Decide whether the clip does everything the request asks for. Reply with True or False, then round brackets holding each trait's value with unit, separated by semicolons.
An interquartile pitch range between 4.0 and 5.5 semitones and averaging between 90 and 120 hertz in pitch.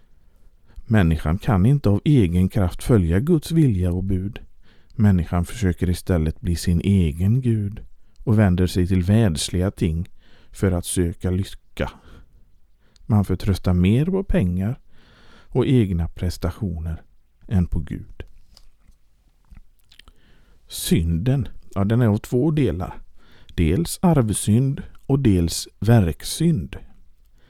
True (4.6 semitones; 95 Hz)